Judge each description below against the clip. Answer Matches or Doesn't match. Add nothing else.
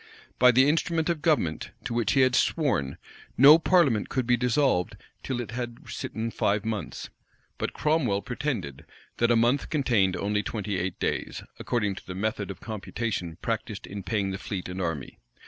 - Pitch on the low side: Matches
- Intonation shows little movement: Doesn't match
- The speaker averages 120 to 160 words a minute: Doesn't match